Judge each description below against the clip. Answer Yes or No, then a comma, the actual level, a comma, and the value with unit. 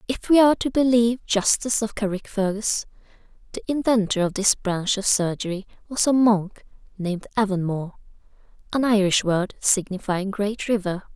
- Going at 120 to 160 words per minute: Yes, slow, 135 wpm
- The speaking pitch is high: Yes, high, 210 Hz